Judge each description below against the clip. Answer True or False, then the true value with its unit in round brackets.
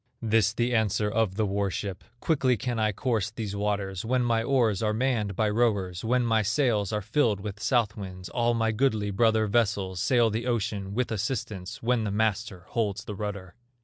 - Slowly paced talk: False (190 wpm)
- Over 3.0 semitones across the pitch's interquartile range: False (2.6 semitones)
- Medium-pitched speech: False (110 Hz)